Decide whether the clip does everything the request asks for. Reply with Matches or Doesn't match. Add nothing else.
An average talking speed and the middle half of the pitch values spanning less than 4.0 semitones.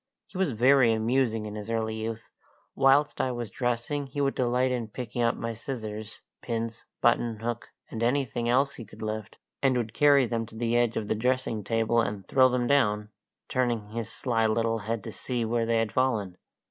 Matches